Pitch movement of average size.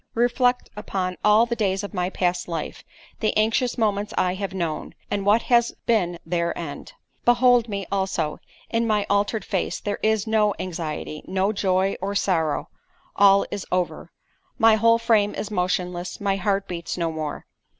Yes: average, 3.4 semitones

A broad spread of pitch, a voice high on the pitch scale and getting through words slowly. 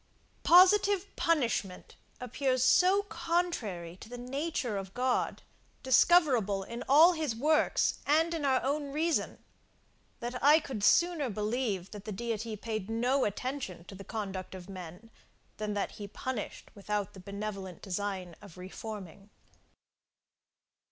Yes: wide, 6.5 semitones; high, 230 Hz; slow, 130 wpm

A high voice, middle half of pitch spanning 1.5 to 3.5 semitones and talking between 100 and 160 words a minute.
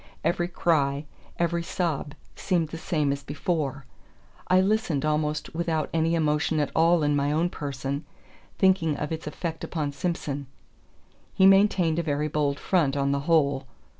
No: medium, 155 Hz; average, 3.0 semitones; average, 155 wpm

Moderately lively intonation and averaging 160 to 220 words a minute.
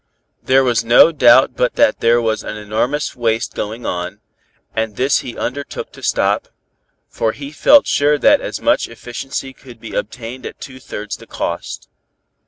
Yes: average, 3.2 semitones; average, 170 wpm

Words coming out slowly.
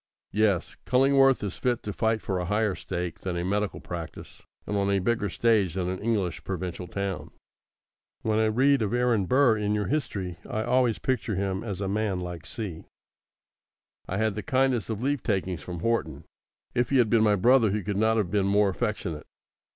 No: average, 195 wpm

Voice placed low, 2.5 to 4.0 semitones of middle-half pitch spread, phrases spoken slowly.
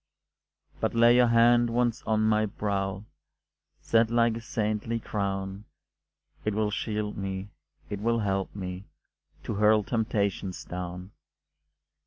Yes: low, 105 Hz; average, 2.8 semitones; slow, 125 wpm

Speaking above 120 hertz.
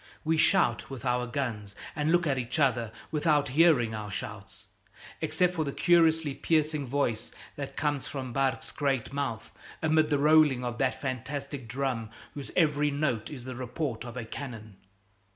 Yes: low, 135 Hz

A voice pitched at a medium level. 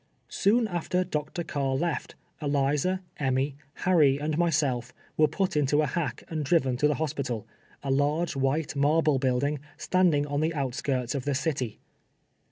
Yes: medium, 145 Hz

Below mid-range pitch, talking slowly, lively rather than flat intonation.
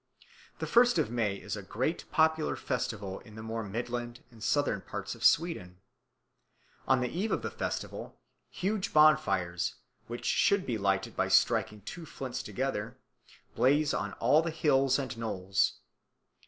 No: low, 120 Hz; average, 155 wpm; wide, 6.6 semitones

